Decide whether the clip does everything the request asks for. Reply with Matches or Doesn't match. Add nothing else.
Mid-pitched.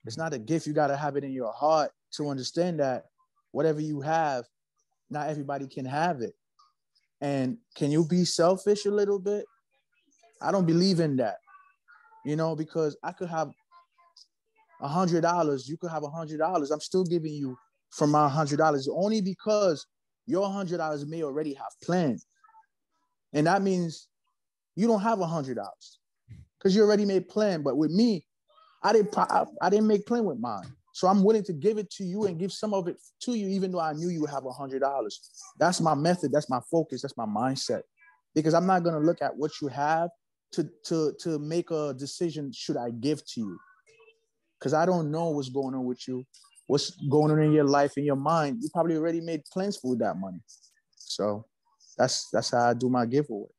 Matches